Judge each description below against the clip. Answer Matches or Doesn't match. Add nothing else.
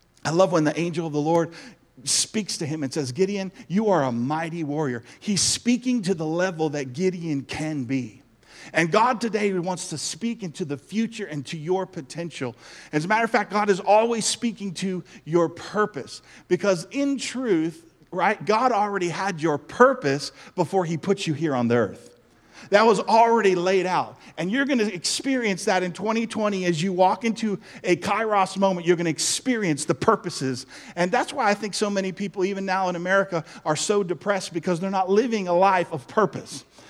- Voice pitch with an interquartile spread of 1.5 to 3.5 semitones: Doesn't match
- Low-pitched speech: Doesn't match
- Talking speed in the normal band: Matches